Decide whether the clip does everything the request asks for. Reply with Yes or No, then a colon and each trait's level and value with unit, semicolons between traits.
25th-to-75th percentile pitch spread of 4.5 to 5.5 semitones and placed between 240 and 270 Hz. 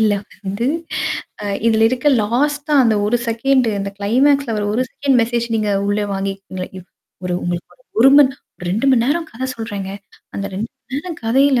No: average, 4.8 semitones; high, 230 Hz